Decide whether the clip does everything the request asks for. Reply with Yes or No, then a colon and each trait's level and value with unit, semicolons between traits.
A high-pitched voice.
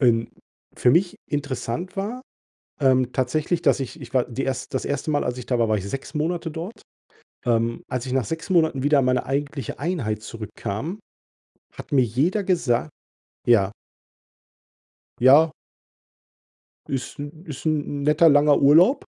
No: medium, 140 Hz